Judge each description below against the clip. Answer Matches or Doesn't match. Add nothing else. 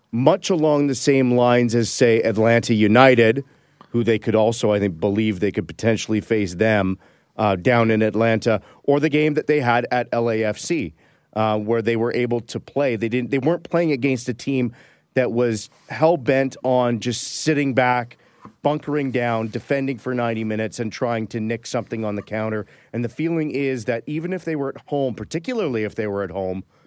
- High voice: Doesn't match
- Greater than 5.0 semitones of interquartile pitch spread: Doesn't match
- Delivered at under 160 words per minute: Doesn't match